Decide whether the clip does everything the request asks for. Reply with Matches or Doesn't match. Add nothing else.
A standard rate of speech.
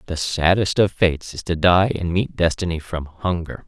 Matches